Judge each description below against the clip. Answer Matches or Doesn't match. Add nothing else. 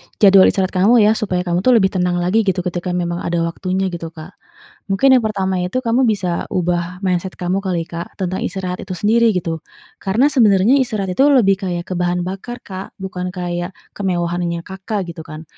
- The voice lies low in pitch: Doesn't match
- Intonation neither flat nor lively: Doesn't match